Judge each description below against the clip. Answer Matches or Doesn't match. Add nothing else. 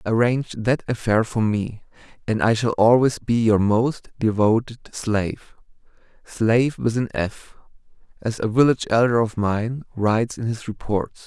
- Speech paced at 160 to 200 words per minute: Doesn't match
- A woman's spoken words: Doesn't match